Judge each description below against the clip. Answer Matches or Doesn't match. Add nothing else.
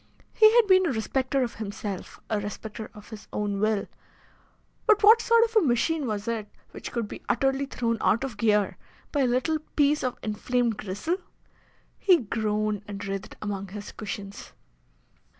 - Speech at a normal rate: Matches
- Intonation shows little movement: Doesn't match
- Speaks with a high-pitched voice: Matches